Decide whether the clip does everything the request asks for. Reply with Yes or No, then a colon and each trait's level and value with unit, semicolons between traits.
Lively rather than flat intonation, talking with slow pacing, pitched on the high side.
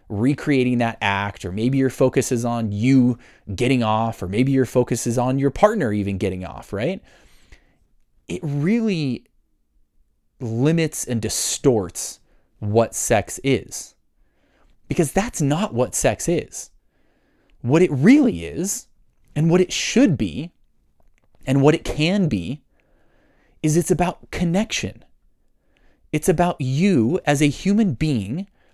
No: wide, 6.5 semitones; slow, 130 wpm; low, 130 Hz